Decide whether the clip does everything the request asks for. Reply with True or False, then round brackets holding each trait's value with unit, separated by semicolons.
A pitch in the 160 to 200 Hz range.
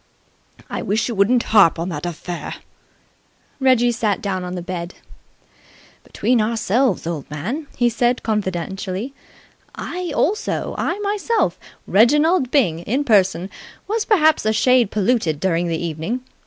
False (215 Hz)